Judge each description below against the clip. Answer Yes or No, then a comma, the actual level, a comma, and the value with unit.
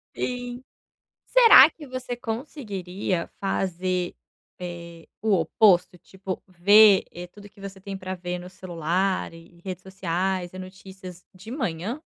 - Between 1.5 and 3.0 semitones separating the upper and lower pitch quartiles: Yes, average, 2.7 semitones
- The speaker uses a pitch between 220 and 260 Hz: No, high, 190 Hz